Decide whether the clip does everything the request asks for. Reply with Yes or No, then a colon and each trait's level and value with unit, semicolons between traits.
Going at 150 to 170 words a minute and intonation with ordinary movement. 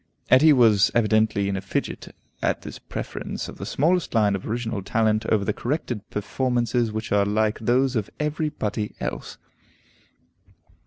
Yes: average, 155 wpm; average, 3.2 semitones